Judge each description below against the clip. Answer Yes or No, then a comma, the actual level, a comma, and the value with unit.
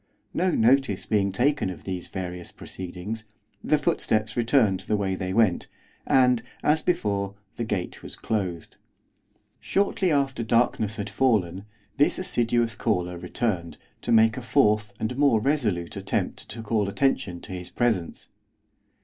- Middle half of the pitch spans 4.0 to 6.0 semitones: Yes, average, 4.7 semitones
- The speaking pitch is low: Yes, low, 110 Hz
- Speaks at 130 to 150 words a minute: Yes, average, 140 wpm